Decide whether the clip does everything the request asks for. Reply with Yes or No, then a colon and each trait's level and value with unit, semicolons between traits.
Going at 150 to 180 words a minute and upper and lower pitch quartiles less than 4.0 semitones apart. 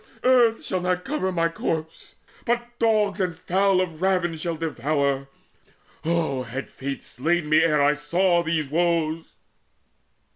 No: average, 140 wpm; average, 3.5 semitones